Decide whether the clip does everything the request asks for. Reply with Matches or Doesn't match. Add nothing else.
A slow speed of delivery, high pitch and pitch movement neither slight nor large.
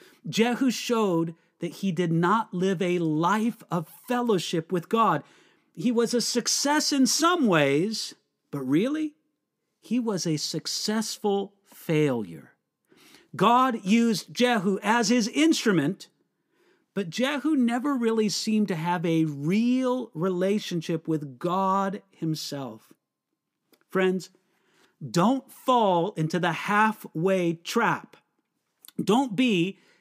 Doesn't match